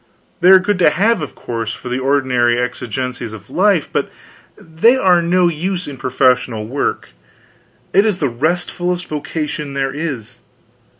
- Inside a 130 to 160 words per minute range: Yes, average, 155 wpm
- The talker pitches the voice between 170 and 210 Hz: No, medium, 150 Hz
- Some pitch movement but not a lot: No, wide, 6.0 semitones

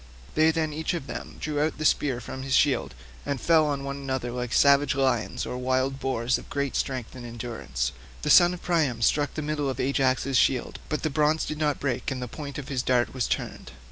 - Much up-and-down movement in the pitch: No, average, 2.9 semitones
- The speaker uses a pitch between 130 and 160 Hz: Yes, low, 135 Hz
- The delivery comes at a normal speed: No, fast, 225 wpm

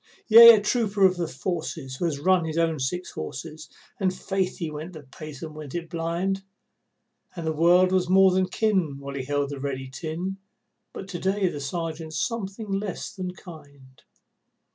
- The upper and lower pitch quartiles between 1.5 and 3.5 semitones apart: No, average, 3.9 semitones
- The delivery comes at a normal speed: Yes, average, 185 wpm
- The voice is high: No, medium, 170 Hz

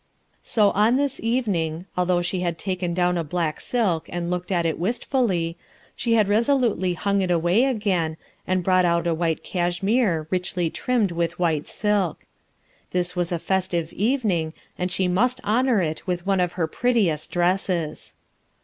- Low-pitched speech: No, medium, 180 Hz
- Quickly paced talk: No, average, 165 wpm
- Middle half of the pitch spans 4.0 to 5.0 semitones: No, average, 3.5 semitones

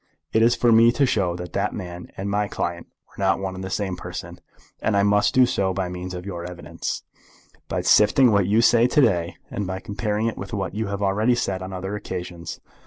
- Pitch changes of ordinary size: Yes, average, 3.1 semitones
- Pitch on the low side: Yes, low, 100 Hz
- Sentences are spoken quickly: Yes, fast, 230 wpm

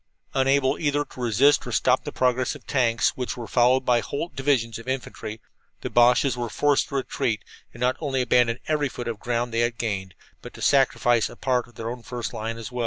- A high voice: No, low, 125 Hz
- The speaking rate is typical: No, fast, 235 wpm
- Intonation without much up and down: Yes, narrow, 2.3 semitones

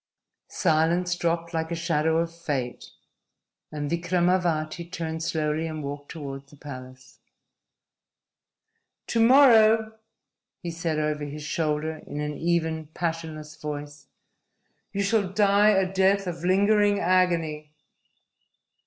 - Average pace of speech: No, slow, 115 wpm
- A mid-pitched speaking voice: Yes, medium, 165 Hz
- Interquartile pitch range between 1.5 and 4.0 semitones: Yes, average, 3.3 semitones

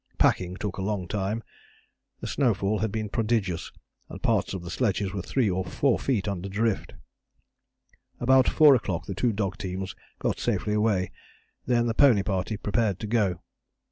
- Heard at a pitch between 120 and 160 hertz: No, low, 105 Hz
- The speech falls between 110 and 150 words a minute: No, average, 170 wpm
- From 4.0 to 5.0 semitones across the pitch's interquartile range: No, average, 3.2 semitones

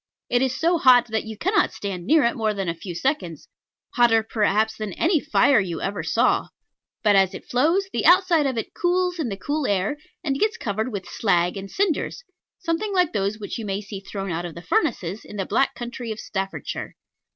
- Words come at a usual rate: No, fast, 210 wpm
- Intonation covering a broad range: Yes, wide, 7.4 semitones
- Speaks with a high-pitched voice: Yes, high, 225 Hz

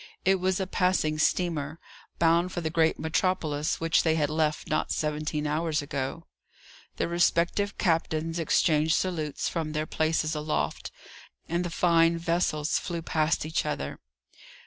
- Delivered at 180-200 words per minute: No, average, 145 wpm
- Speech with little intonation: Yes, narrow, 1.9 semitones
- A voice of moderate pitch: Yes, medium, 160 Hz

